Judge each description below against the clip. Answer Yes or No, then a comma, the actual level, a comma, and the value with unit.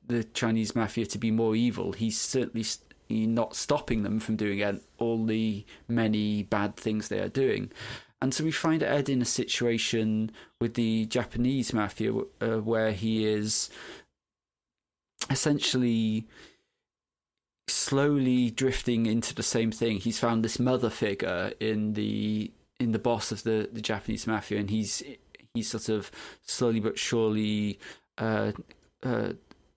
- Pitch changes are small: Yes, narrow, 1.8 semitones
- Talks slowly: No, average, 145 wpm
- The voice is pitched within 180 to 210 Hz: No, low, 110 Hz